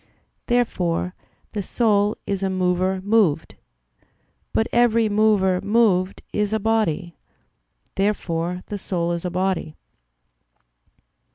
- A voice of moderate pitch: No, high, 195 Hz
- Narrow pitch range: No, average, 3.1 semitones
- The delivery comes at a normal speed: No, slow, 105 wpm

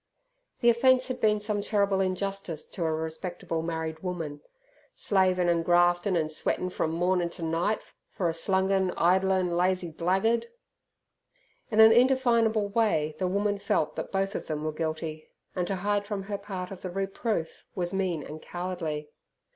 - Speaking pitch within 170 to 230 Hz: Yes, medium, 185 Hz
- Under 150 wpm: No, average, 165 wpm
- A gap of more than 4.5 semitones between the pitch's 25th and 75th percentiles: No, average, 3.4 semitones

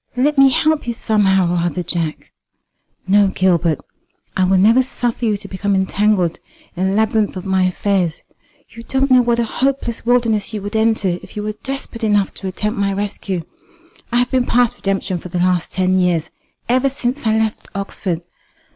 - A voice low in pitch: No, high, 205 Hz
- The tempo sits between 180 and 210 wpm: Yes, average, 185 wpm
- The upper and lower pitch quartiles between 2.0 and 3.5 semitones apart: No, average, 4.1 semitones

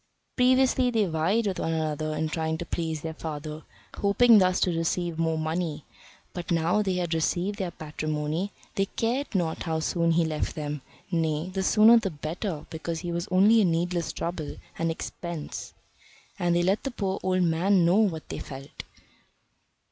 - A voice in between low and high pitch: Yes, medium, 170 Hz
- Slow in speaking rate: No, average, 175 wpm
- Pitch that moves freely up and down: No, average, 3.2 semitones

